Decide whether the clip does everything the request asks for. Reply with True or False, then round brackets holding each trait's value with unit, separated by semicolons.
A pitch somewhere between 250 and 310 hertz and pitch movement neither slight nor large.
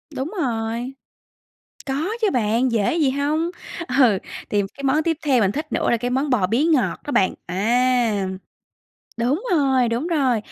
True (255 Hz; 4.0 semitones)